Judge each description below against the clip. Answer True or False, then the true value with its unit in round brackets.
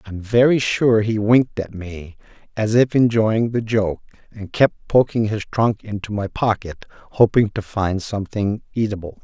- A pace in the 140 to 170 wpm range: True (160 wpm)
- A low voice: True (105 Hz)